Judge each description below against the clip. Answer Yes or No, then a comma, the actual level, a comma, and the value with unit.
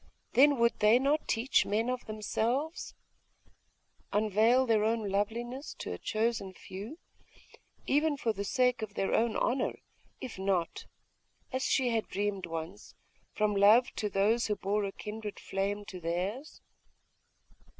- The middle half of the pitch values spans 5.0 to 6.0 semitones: No, average, 3.5 semitones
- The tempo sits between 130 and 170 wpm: Yes, average, 140 wpm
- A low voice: No, high, 220 Hz